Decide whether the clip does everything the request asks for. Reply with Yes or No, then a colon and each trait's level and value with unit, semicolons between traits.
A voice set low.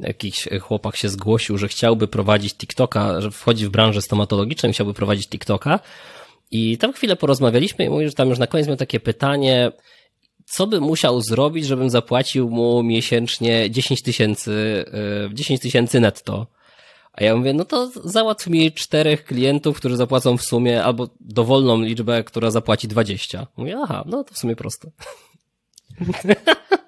Yes: low, 120 Hz